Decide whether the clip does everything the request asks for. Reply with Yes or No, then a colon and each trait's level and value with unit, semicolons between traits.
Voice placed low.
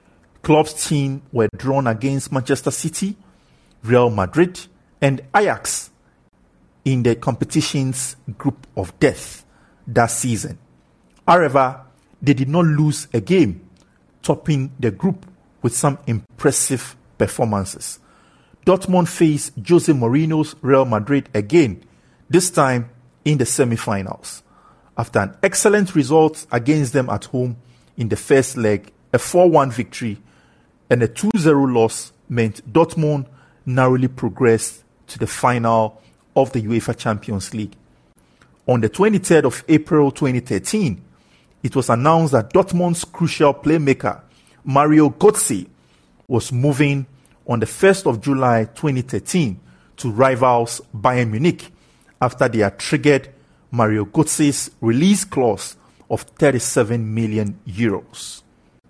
Yes: low, 130 Hz